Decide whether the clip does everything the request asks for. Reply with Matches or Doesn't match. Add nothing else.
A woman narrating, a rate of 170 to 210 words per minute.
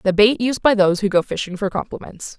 Doesn't match